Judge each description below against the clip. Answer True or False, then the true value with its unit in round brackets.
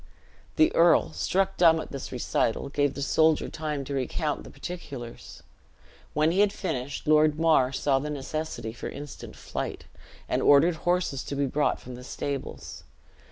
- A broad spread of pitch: False (3.2 semitones)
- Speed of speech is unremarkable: True (160 wpm)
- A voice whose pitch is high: False (145 Hz)